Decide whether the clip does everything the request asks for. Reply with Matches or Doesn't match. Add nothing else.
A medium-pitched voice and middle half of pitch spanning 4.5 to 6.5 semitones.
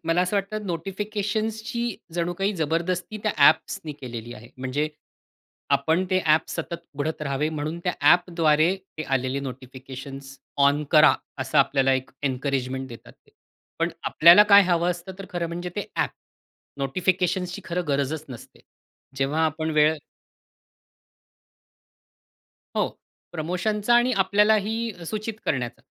Matches